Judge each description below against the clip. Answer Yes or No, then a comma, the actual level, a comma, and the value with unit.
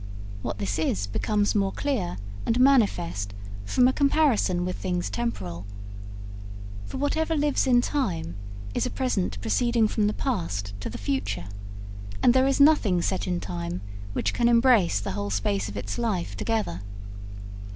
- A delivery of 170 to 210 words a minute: No, average, 155 wpm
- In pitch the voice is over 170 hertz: Yes, high, 190 Hz